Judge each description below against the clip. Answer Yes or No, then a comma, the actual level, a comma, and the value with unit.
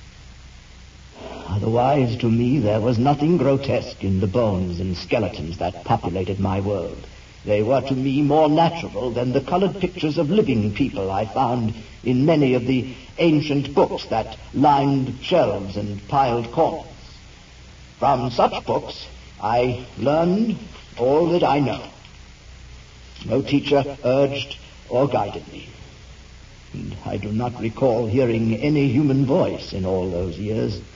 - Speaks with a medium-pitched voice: No, low, 120 Hz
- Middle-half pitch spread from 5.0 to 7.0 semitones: Yes, wide, 5.6 semitones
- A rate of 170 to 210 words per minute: No, average, 140 wpm